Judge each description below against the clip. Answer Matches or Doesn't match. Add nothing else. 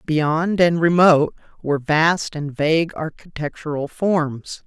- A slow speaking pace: Matches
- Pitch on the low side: Doesn't match